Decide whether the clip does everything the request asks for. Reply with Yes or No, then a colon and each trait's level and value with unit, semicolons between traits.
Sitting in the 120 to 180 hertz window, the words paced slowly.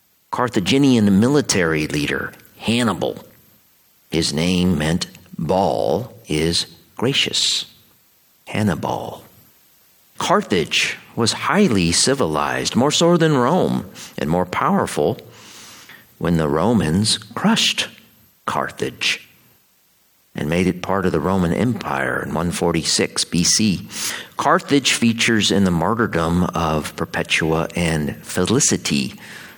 No: very low, 90 Hz; slow, 100 wpm